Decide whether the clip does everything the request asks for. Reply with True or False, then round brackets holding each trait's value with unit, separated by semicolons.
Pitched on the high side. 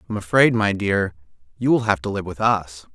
False (100 Hz)